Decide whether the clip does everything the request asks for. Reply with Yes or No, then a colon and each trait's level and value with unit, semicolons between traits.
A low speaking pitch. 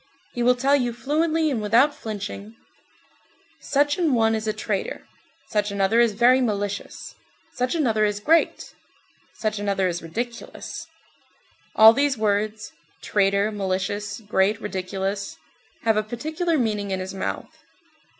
No: high, 215 Hz